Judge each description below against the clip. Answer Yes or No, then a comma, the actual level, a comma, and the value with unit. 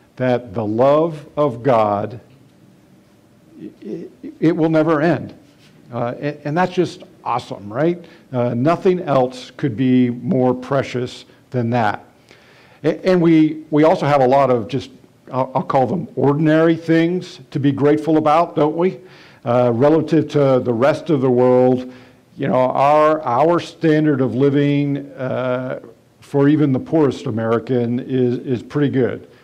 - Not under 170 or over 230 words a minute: No, average, 150 wpm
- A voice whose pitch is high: No, medium, 140 Hz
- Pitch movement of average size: Yes, average, 3.7 semitones